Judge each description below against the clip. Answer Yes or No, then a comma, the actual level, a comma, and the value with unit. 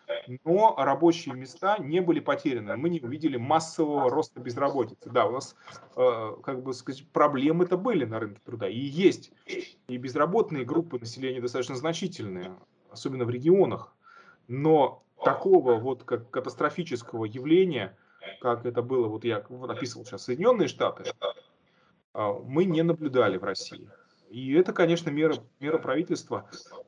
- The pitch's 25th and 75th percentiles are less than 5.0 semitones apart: No, wide, 5.6 semitones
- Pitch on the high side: No, medium, 140 Hz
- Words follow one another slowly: No, average, 140 wpm